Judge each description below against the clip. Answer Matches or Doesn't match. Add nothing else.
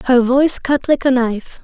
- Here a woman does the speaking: Matches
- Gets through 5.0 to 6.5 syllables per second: Matches